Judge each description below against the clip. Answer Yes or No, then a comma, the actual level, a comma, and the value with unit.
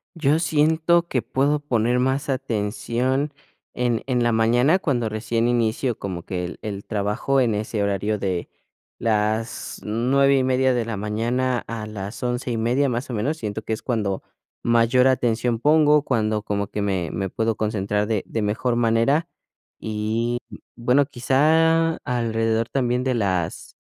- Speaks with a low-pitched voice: Yes, low, 120 Hz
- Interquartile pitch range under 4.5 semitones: Yes, average, 3.5 semitones